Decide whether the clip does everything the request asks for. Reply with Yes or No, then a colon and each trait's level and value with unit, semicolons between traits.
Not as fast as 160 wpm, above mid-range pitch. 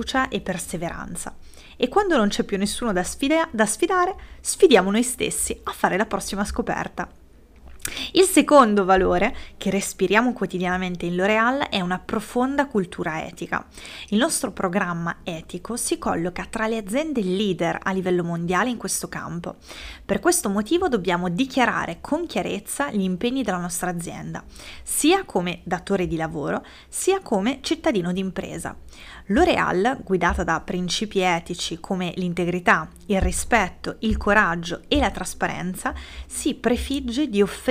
Yes: average, 140 wpm; high, 200 Hz